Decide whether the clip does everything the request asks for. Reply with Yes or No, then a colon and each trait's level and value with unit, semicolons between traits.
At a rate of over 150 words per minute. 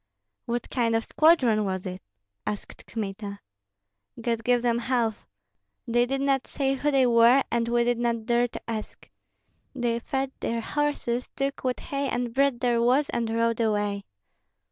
Yes: average, 165 wpm